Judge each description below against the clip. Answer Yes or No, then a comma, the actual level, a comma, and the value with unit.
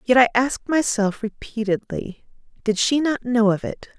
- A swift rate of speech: No, average, 165 wpm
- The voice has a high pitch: Yes, high, 230 Hz